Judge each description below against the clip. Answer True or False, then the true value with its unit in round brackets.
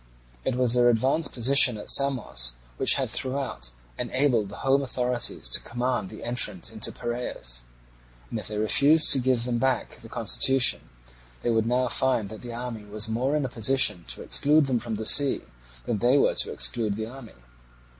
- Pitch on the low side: True (120 Hz)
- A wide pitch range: False (3.3 semitones)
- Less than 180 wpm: False (185 wpm)